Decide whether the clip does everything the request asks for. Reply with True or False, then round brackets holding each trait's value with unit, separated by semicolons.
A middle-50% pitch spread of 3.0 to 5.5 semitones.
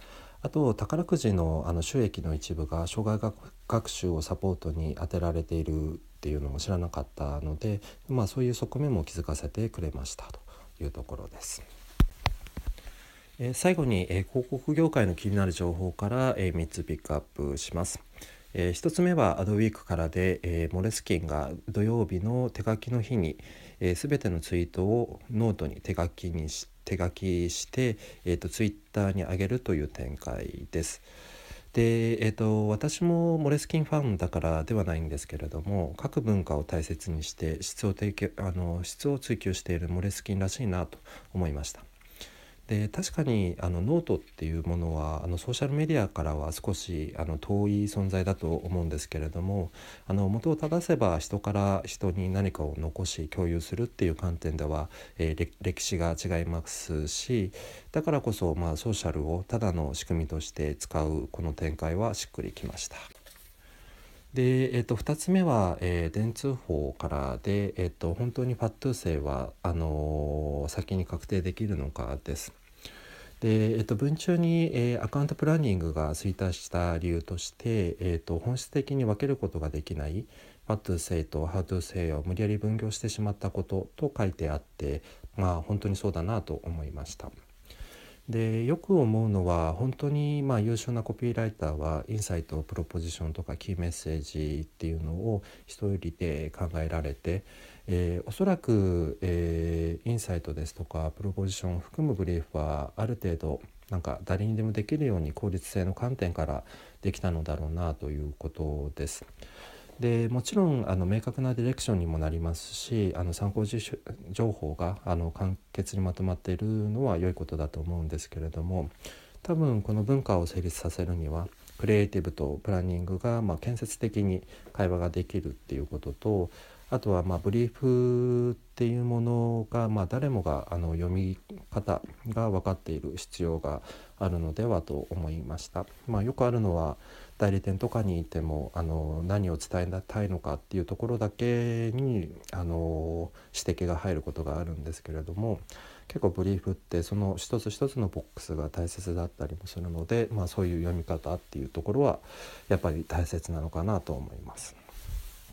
True (5.2 semitones)